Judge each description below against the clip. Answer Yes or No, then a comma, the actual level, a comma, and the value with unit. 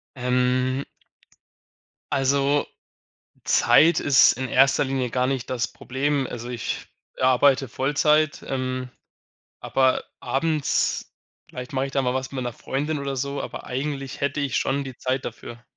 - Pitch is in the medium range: No, low, 130 Hz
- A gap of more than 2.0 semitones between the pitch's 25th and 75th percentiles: No, narrow, 1.7 semitones